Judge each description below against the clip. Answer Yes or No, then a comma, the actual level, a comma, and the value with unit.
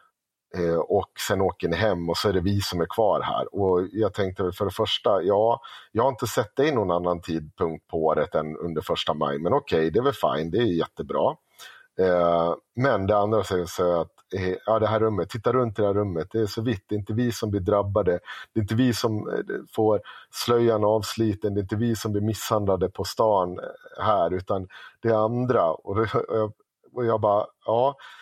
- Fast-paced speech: Yes, fast, 205 wpm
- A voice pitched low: Yes, low, 105 Hz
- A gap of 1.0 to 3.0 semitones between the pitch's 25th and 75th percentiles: No, average, 3.4 semitones